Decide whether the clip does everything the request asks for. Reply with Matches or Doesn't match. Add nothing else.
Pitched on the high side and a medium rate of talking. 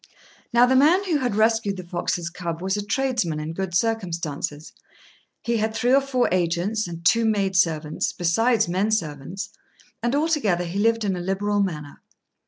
Matches